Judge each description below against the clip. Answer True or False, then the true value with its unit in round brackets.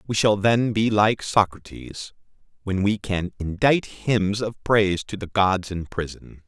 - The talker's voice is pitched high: False (100 Hz)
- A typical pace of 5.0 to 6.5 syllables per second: False (4.2 syllables/s)